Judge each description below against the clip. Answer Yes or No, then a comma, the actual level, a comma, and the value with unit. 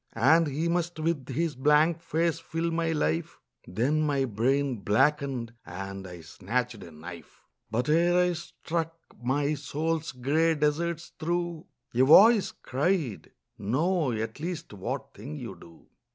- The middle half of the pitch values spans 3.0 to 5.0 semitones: No, wide, 5.4 semitones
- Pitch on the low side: No, medium, 150 Hz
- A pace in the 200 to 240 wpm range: No, average, 140 wpm